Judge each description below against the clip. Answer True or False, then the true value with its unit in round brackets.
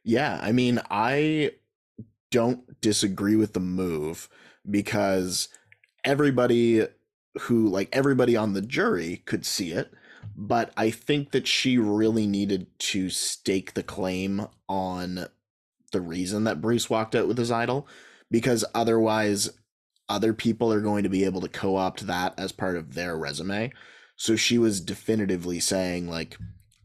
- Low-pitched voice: True (105 Hz)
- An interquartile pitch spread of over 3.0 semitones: True (3.4 semitones)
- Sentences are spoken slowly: False (145 wpm)